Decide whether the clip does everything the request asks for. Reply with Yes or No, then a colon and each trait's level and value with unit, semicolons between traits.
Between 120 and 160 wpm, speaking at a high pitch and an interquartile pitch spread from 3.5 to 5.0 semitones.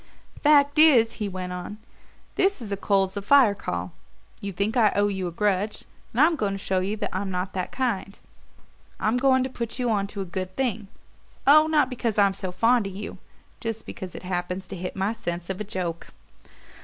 No: fast, 205 wpm; high, 205 Hz; average, 4.2 semitones